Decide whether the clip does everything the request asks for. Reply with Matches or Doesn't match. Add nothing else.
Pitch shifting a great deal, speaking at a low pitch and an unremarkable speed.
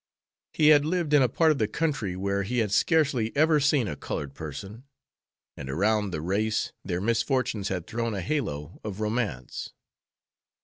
Matches